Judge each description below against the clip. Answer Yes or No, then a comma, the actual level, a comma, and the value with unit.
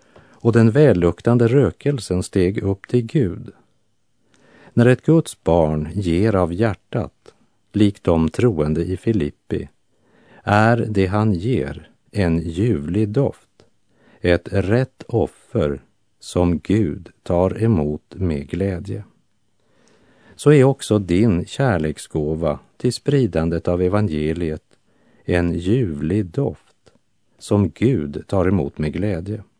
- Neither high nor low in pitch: No, low, 100 Hz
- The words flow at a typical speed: No, slow, 110 wpm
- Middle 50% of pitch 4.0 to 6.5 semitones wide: Yes, average, 5.2 semitones